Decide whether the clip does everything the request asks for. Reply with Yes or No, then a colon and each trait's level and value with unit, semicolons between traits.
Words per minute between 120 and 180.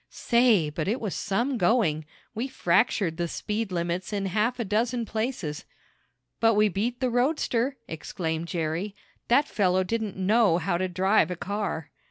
Yes: average, 160 wpm